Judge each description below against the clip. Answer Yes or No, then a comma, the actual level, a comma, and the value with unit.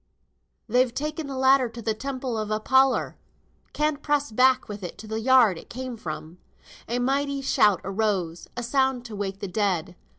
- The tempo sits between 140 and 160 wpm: No, average, 175 wpm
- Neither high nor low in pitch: No, high, 235 Hz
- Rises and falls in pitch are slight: No, average, 4.3 semitones